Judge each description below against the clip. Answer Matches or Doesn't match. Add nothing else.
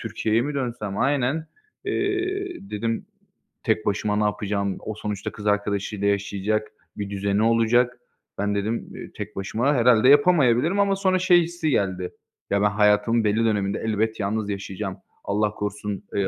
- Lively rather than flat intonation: Doesn't match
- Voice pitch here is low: Matches